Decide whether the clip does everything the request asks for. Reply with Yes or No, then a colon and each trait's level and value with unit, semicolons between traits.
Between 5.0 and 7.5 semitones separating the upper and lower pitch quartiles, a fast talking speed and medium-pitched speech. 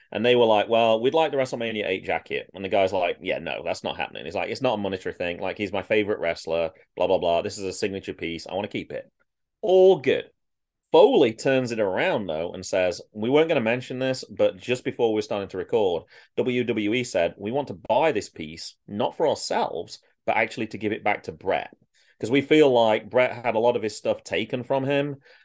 No: wide, 5.5 semitones; fast, 235 wpm; low, 120 Hz